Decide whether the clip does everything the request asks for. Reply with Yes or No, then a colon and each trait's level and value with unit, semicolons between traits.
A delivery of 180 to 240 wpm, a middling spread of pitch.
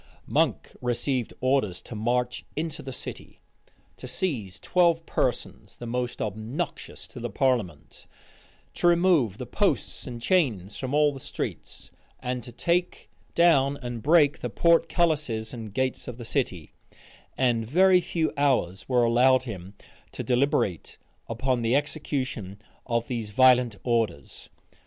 No: average, 140 wpm; average, 4.0 semitones